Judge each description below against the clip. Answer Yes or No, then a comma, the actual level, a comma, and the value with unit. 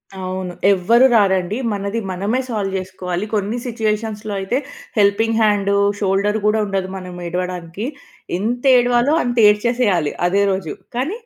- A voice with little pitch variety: No, average, 3.1 semitones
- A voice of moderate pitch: No, high, 200 Hz